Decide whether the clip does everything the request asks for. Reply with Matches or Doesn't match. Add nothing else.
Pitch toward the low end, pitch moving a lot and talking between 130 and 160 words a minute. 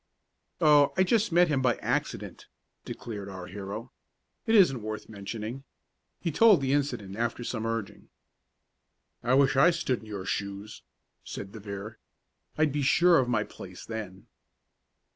Matches